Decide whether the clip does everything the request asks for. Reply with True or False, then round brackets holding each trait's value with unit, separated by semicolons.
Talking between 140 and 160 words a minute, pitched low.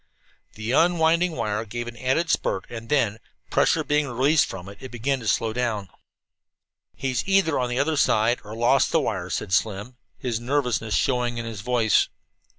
False (175 wpm; 120 Hz)